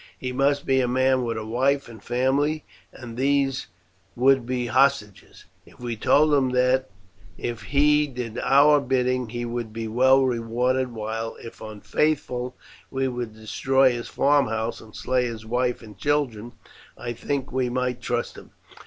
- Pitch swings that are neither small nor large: No, narrow, 2.3 semitones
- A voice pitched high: No, low, 125 Hz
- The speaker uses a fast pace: No, average, 160 wpm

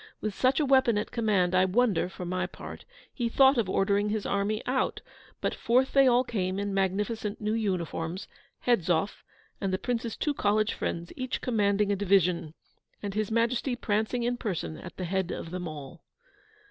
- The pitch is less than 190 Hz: No, high, 205 Hz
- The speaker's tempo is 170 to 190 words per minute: Yes, average, 180 wpm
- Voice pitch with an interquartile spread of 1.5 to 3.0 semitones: No, average, 4.1 semitones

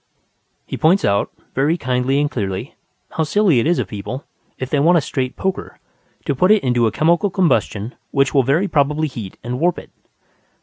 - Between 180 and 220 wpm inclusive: Yes, average, 190 wpm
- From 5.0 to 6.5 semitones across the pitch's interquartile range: Yes, average, 5.3 semitones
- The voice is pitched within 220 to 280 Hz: No, medium, 140 Hz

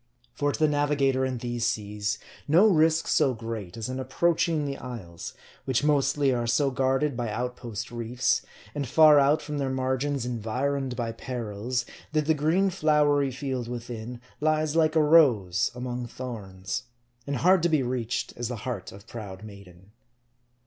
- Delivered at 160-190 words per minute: Yes, average, 165 wpm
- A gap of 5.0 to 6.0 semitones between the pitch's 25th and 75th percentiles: No, average, 3.9 semitones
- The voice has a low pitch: Yes, low, 130 Hz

